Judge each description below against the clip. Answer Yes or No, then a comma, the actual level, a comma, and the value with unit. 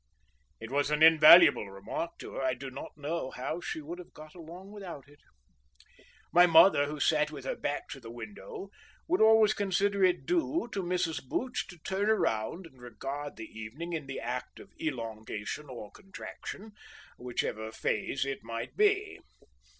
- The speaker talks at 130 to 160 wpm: No, average, 170 wpm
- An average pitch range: No, wide, 6.6 semitones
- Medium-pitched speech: Yes, medium, 150 Hz